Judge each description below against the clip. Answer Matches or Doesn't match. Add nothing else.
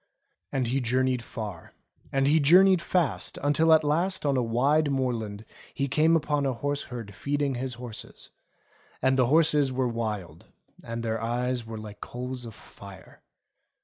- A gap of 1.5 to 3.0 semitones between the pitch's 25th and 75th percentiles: Doesn't match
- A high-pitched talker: Doesn't match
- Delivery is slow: Doesn't match